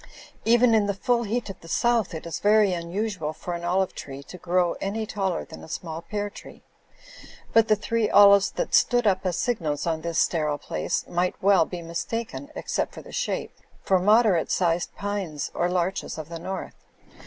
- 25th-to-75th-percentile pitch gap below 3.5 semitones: No, average, 3.9 semitones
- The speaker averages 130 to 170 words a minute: No, average, 190 wpm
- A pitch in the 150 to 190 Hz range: Yes, medium, 185 Hz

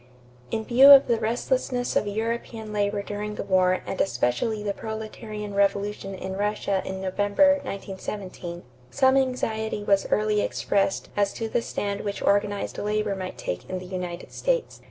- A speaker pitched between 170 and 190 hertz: No, high, 205 Hz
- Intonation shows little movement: Yes, narrow, 2.2 semitones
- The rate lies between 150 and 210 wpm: Yes, average, 160 wpm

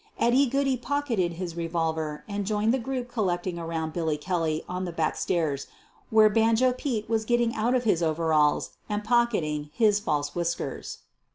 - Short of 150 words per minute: No, average, 170 wpm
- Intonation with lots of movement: Yes, wide, 6.2 semitones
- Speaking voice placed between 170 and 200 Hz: Yes, high, 190 Hz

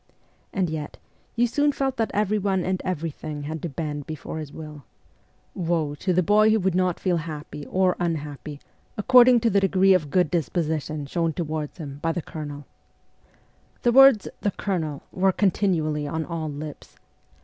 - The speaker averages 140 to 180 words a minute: No, average, 195 wpm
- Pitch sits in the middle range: Yes, medium, 170 Hz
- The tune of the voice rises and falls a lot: No, average, 4.1 semitones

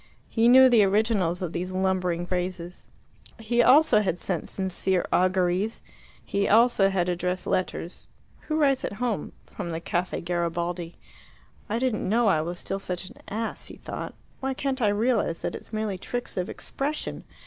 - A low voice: No, high, 190 Hz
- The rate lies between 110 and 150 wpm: No, average, 165 wpm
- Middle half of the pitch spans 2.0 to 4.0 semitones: No, average, 4.4 semitones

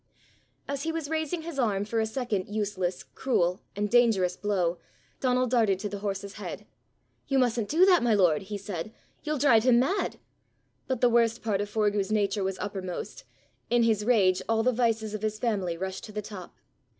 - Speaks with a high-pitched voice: Yes, high, 215 Hz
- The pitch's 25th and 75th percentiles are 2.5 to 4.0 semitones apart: Yes, average, 3.6 semitones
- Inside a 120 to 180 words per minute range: No, average, 190 wpm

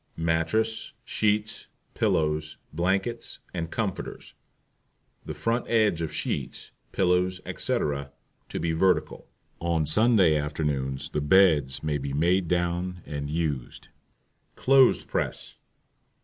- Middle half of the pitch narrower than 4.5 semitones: Yes, average, 4.1 semitones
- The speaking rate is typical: No, slow, 105 wpm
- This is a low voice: Yes, very low, 85 Hz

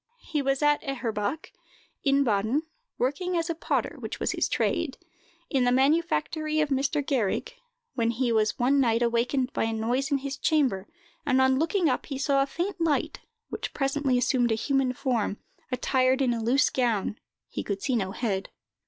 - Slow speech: No, average, 180 wpm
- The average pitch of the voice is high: Yes, very high, 265 Hz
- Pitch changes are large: No, average, 3.5 semitones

